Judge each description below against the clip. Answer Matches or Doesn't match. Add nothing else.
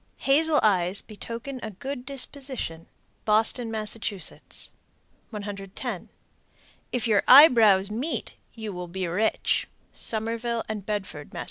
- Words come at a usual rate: Doesn't match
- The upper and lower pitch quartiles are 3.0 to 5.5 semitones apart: Matches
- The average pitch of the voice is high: Matches